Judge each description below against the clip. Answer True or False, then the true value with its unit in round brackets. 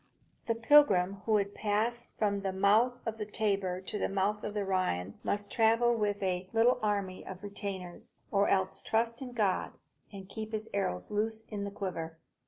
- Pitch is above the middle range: True (205 Hz)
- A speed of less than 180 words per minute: False (185 wpm)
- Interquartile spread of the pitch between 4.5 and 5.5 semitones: False (2.5 semitones)